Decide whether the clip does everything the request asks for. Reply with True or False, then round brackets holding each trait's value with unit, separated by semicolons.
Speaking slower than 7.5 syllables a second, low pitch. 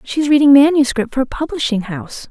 False (6.3 syllables/s; 270 Hz)